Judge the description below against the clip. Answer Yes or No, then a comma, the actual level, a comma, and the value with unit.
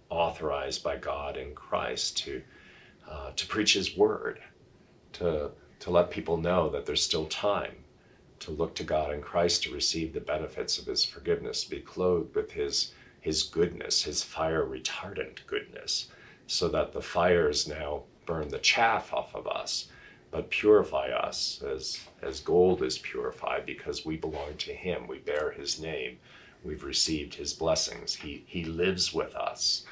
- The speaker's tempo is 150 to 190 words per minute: Yes, average, 160 wpm